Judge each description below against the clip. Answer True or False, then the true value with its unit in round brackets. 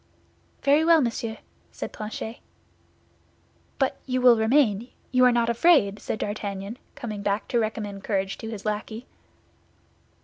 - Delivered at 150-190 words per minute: False (135 wpm)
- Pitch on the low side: False (225 Hz)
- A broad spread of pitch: False (3.2 semitones)